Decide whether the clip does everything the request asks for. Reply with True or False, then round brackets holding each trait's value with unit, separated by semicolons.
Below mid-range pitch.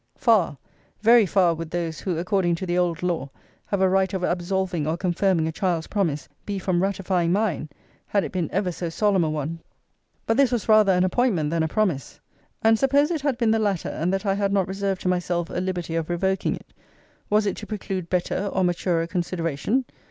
False (185 Hz)